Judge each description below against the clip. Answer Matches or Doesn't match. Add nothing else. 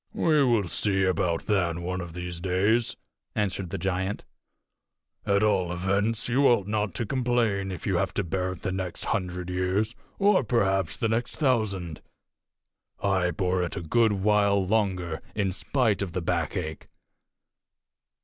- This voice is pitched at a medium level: Doesn't match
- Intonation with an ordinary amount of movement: Matches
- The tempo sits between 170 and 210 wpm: Doesn't match